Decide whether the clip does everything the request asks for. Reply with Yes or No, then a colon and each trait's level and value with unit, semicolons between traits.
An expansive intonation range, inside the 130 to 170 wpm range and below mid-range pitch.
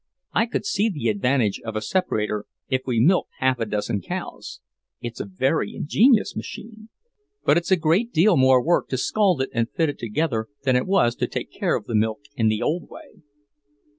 No: wide, 8.1 semitones; average, 200 wpm; low, 130 Hz